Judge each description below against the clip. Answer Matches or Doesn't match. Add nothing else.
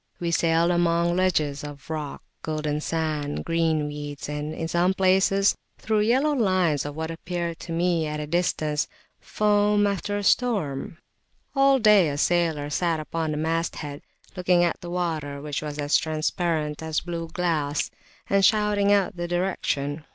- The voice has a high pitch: Doesn't match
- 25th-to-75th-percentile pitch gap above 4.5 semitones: Doesn't match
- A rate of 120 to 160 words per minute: Matches